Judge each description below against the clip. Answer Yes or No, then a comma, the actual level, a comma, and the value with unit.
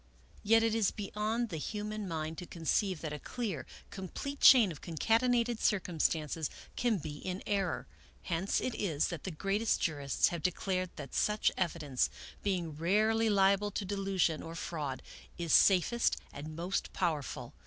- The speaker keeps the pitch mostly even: No, average, 4.6 semitones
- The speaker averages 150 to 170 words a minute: Yes, average, 155 wpm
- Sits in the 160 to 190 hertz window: Yes, medium, 185 Hz